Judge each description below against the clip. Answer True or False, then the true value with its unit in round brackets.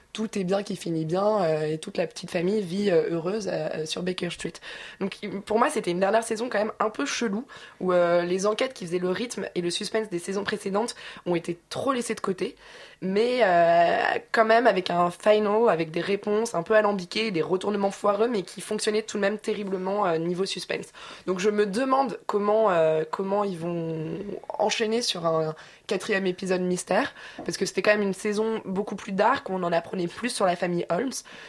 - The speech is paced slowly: False (210 wpm)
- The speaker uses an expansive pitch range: False (3.5 semitones)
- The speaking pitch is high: True (200 Hz)